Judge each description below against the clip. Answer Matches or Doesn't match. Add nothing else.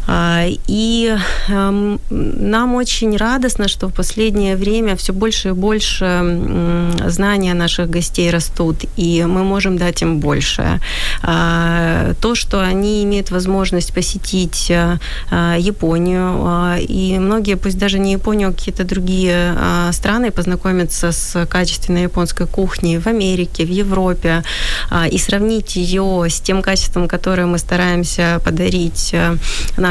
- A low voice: Doesn't match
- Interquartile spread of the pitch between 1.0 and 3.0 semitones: Matches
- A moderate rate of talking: Matches